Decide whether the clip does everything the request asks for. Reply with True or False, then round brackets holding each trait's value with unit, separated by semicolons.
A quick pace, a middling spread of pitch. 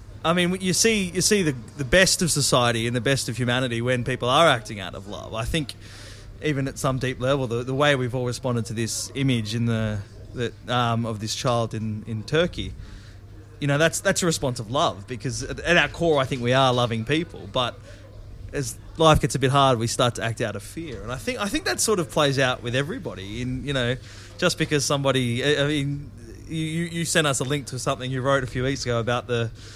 True (240 wpm; 4.4 semitones)